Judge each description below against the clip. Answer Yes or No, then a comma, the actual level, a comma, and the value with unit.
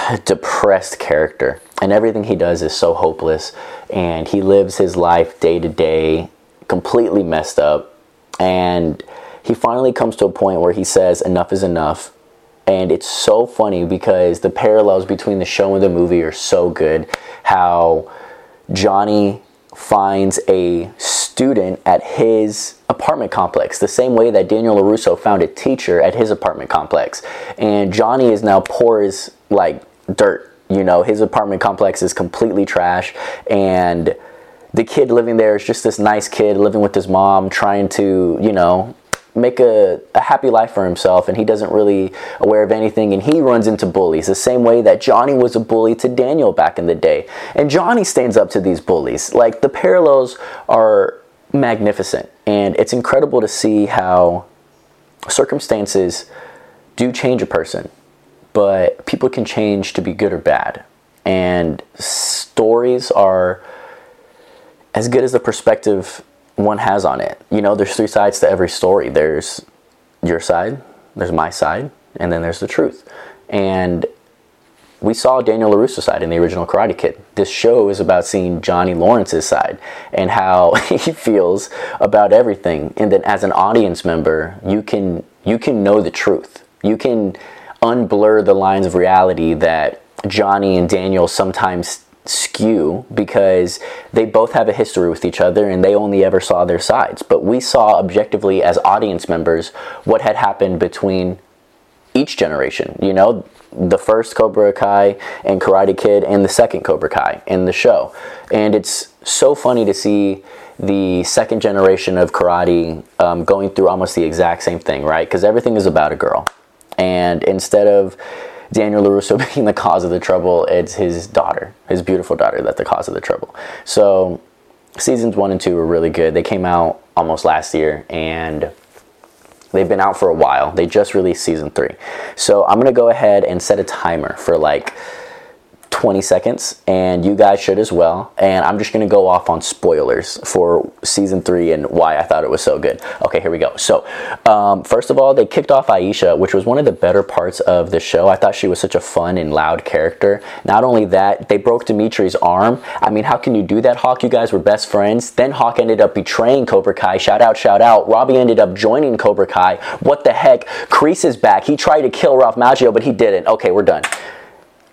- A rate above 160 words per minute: Yes, average, 180 wpm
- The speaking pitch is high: No, low, 100 Hz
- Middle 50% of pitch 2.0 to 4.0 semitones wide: No, wide, 5.6 semitones